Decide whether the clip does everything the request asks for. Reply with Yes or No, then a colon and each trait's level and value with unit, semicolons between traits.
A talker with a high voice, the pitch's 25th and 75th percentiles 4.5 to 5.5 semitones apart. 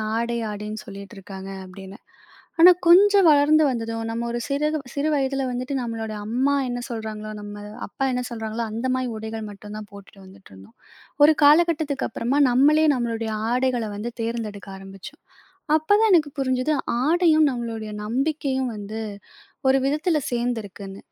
Yes: high, 235 Hz; average, 4.8 semitones